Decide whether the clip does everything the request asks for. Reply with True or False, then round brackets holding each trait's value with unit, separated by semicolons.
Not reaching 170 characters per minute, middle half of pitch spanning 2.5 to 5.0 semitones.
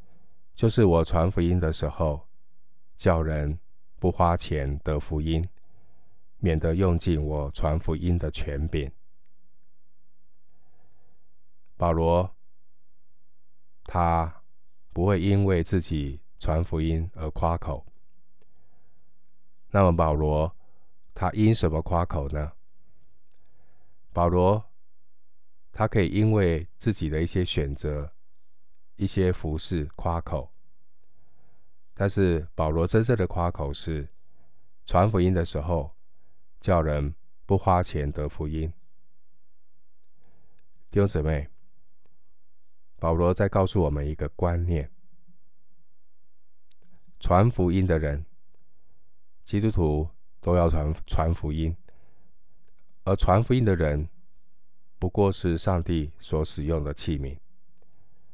True (150 characters per minute; 2.8 semitones)